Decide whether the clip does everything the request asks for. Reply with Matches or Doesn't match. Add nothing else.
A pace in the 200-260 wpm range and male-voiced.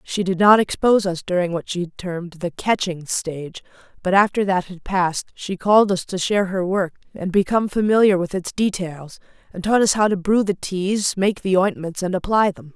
Doesn't match